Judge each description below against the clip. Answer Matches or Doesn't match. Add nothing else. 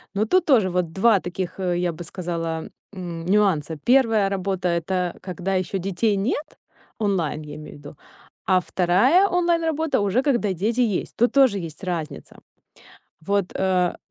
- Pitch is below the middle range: Doesn't match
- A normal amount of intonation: Matches